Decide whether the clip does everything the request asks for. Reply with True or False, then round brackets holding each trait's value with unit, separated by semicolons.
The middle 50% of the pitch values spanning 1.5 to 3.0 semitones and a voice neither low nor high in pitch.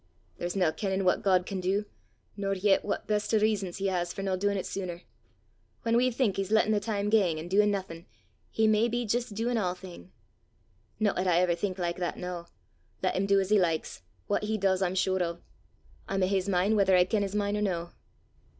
False (2.5 semitones; 195 Hz)